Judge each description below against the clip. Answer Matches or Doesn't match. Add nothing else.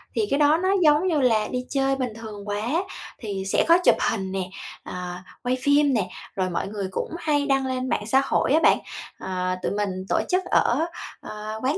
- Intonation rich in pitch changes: Matches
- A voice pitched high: Matches